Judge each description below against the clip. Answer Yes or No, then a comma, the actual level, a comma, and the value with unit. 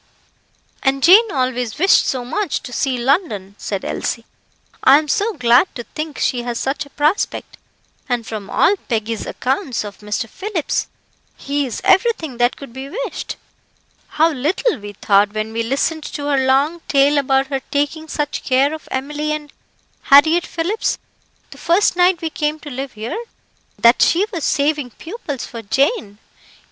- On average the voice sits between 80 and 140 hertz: No, very high, 280 Hz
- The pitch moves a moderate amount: Yes, average, 4.6 semitones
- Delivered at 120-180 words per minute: Yes, average, 165 wpm